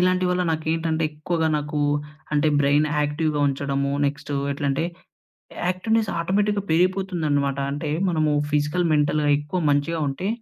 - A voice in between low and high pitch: Yes, medium, 155 Hz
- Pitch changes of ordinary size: Yes, average, 3.5 semitones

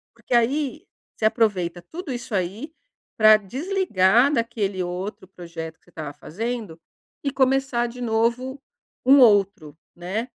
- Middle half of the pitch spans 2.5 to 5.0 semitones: No, wide, 5.5 semitones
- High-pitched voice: Yes, high, 225 Hz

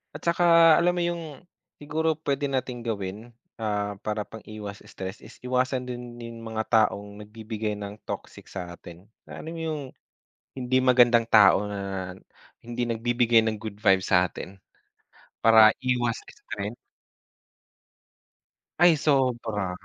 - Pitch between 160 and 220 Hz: No, low, 115 Hz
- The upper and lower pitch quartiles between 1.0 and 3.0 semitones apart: No, average, 3.8 semitones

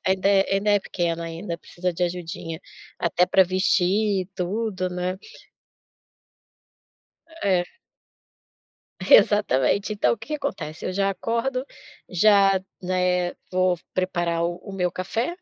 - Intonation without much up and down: Yes, narrow, 2.3 semitones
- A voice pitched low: No, medium, 185 Hz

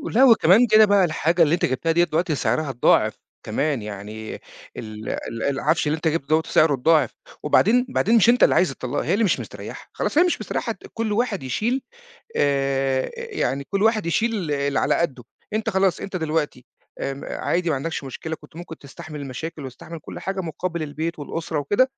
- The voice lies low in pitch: No, medium, 160 Hz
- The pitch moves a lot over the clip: Yes, wide, 5.9 semitones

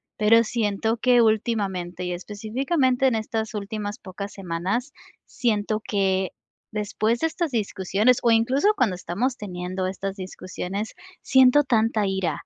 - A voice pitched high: Yes, high, 215 Hz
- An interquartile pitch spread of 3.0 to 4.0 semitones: Yes, average, 3.6 semitones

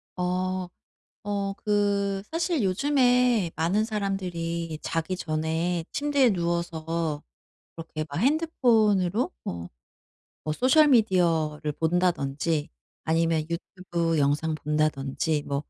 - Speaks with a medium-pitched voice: Yes, medium, 175 Hz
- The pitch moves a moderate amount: Yes, average, 4.5 semitones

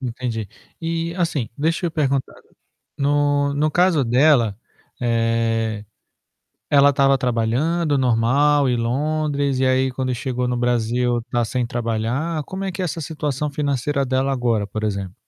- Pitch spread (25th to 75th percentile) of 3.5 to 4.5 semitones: Yes, average, 3.8 semitones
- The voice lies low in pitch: Yes, low, 130 Hz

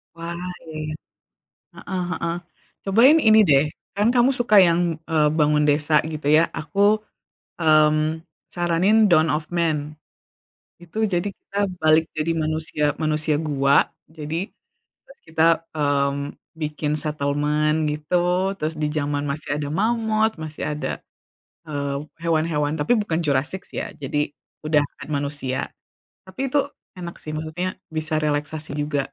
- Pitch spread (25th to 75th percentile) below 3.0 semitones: Yes, narrow, 2.4 semitones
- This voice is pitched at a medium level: Yes, medium, 155 Hz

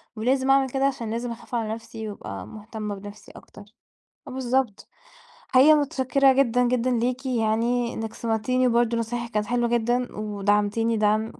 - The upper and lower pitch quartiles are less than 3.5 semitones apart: Yes, average, 2.7 semitones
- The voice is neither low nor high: No, high, 235 Hz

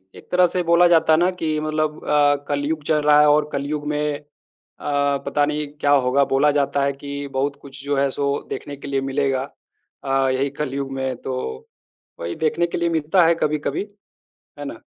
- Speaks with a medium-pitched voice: Yes, medium, 145 Hz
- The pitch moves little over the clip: Yes, narrow, 1.8 semitones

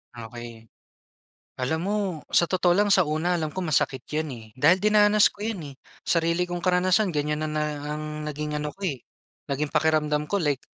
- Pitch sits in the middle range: Yes, medium, 155 Hz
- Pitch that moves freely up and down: No, average, 3.5 semitones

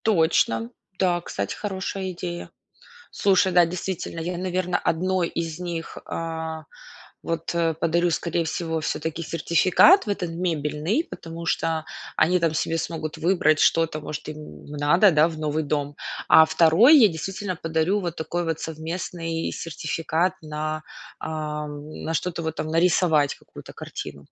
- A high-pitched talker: No, medium, 165 Hz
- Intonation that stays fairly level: Yes, narrow, 2.1 semitones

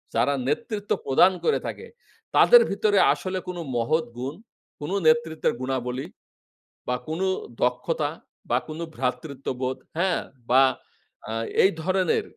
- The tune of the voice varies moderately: No, wide, 6.3 semitones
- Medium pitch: Yes, medium, 155 Hz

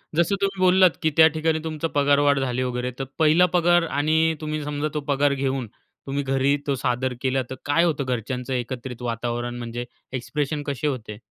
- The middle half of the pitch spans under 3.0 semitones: No, average, 3.7 semitones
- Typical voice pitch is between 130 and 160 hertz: Yes, medium, 140 Hz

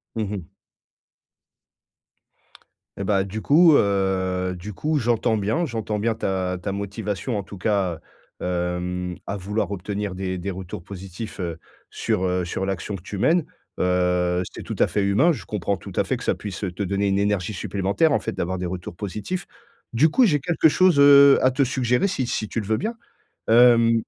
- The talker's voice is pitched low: Yes, low, 100 Hz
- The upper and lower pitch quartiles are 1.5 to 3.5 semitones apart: No, average, 4.2 semitones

